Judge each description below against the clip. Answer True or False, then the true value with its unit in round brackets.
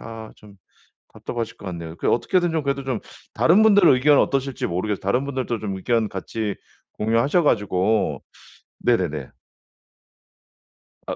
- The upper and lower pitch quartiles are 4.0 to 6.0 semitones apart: True (5.3 semitones)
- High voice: False (115 Hz)